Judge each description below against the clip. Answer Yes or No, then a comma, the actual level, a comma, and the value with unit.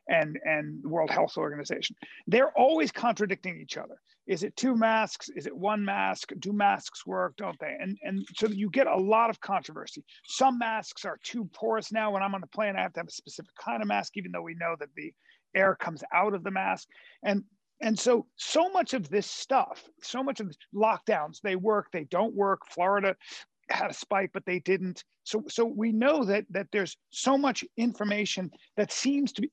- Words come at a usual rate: No, fast, 210 wpm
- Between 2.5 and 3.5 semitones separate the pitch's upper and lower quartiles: Yes, average, 3.2 semitones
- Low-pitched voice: No, high, 205 Hz